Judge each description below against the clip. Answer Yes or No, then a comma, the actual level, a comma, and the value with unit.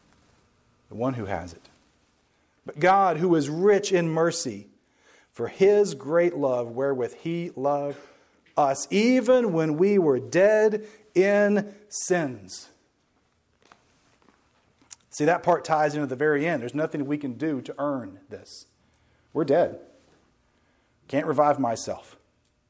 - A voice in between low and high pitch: Yes, medium, 155 Hz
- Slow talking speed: Yes, slow, 125 wpm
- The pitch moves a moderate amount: No, wide, 6.1 semitones